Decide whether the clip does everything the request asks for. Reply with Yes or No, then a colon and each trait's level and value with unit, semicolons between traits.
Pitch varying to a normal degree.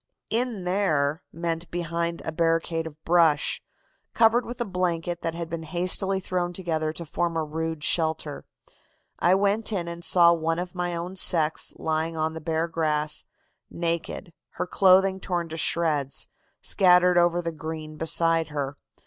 No: narrow, 1.9 semitones